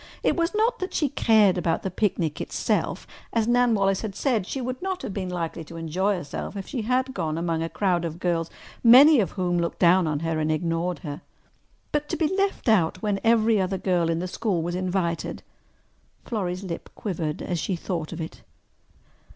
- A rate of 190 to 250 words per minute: Yes, average, 200 wpm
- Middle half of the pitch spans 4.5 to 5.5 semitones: Yes, average, 5.2 semitones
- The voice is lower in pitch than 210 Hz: Yes, medium, 185 Hz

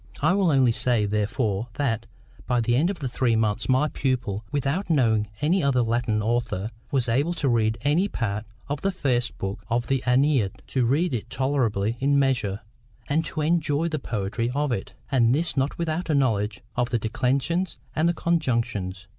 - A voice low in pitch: Yes, low, 125 Hz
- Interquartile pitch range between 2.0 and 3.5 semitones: No, average, 4.5 semitones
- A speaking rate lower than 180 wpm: Yes, average, 170 wpm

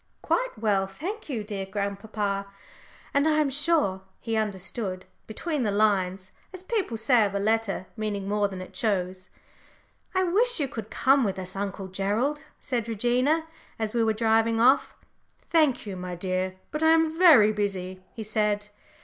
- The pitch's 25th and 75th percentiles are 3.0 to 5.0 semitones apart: No, wide, 5.6 semitones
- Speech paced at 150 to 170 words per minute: Yes, average, 165 wpm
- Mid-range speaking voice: No, high, 215 Hz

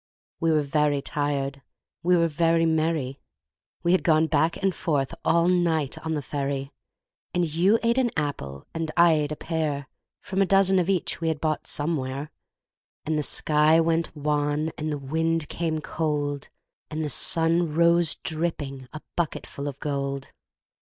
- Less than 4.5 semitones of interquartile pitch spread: Yes, narrow, 2.4 semitones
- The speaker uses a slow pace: No, average, 165 wpm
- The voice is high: No, medium, 155 Hz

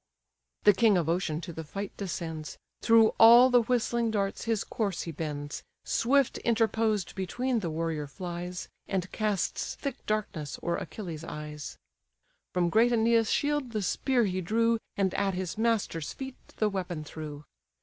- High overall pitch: Yes, high, 195 Hz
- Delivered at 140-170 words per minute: Yes, average, 155 wpm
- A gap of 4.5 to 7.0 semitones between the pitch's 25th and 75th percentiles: Yes, wide, 5.4 semitones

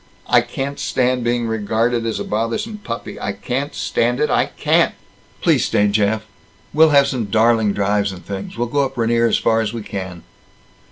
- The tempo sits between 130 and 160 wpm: No, average, 185 wpm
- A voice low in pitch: Yes, low, 115 Hz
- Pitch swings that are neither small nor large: Yes, average, 3.3 semitones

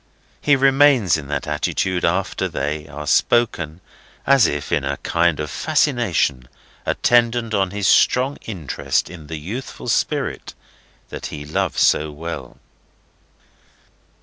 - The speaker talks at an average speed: No, slow, 125 wpm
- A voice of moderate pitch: No, very low, 85 Hz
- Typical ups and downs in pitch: No, wide, 7.7 semitones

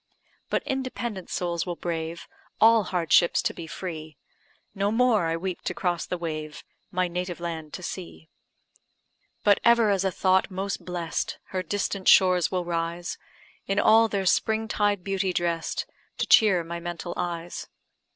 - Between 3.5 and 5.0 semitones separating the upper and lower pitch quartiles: No, average, 2.8 semitones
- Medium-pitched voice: Yes, medium, 180 Hz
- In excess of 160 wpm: No, average, 155 wpm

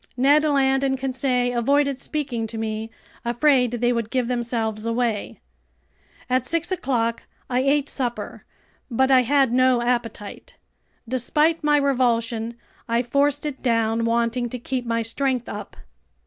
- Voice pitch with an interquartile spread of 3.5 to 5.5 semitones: No, average, 2.8 semitones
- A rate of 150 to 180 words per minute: No, average, 140 wpm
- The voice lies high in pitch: Yes, very high, 250 Hz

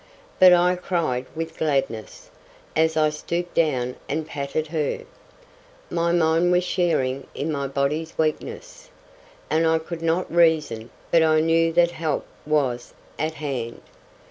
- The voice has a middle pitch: Yes, medium, 160 Hz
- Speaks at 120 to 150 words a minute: Yes, average, 140 wpm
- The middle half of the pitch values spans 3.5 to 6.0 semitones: No, average, 3.0 semitones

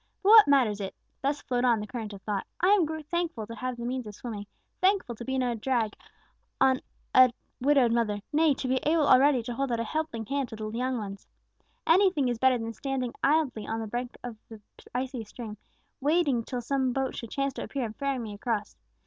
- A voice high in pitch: Yes, very high, 250 Hz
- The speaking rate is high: Yes, fast, 215 wpm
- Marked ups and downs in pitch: No, average, 3.5 semitones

